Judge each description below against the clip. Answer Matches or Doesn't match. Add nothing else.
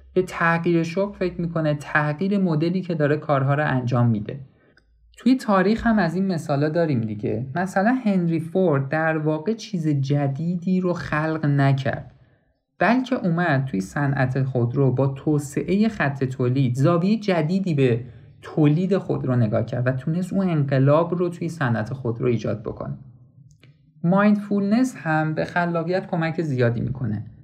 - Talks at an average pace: Matches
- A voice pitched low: Doesn't match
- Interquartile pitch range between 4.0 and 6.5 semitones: Matches